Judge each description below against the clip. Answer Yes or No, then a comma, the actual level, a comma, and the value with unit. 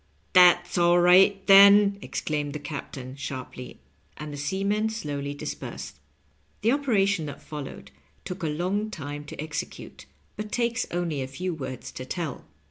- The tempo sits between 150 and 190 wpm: Yes, average, 160 wpm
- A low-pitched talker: No, medium, 170 Hz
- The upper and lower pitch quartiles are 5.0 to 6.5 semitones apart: Yes, wide, 5.6 semitones